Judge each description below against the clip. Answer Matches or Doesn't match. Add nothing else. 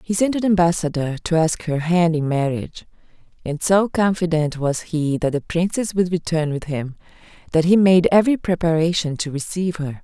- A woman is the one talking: Matches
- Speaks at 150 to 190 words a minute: Matches